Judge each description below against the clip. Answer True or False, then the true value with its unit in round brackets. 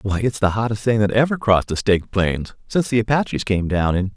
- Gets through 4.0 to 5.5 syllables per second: False (6.1 syllables/s)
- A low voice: True (105 Hz)